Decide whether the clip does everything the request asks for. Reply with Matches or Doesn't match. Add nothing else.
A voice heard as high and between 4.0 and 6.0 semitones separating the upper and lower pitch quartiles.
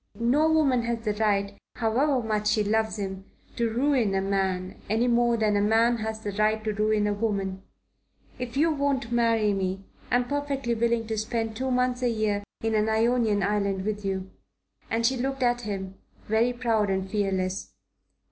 Doesn't match